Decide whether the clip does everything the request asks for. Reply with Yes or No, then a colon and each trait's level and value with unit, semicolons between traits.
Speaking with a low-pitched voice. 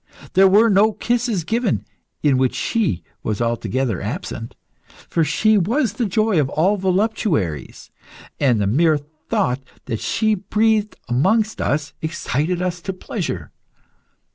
No: medium, 180 Hz